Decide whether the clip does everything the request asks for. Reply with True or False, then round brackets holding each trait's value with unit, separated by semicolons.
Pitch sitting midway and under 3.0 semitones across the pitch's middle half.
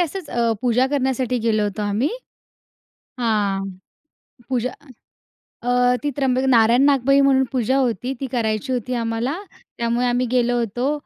False (245 Hz; 2.6 semitones)